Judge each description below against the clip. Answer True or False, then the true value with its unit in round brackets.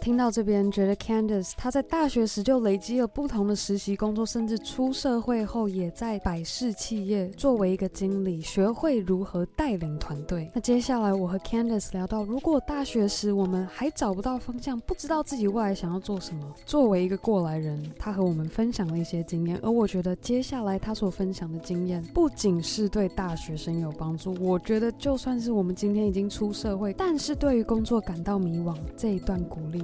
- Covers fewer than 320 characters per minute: False (335 characters per minute)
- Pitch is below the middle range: False (205 Hz)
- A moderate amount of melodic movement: True (4.3 semitones)